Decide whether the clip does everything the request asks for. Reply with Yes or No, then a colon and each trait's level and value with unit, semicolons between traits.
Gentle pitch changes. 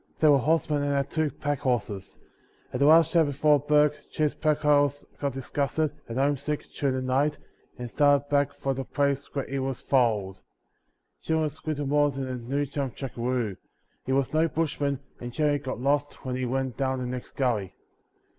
Yes: narrow, 2.3 semitones